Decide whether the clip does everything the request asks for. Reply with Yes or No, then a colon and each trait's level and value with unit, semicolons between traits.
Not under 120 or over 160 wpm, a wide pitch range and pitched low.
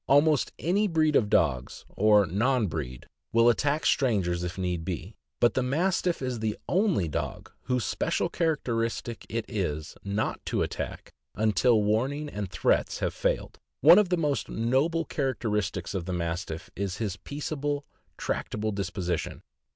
Yes: average, 150 wpm; wide, 7.3 semitones; low, 115 Hz